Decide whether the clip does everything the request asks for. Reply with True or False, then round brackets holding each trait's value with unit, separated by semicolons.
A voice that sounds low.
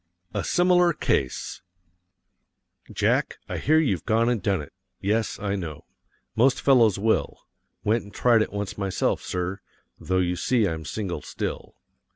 True (105 Hz)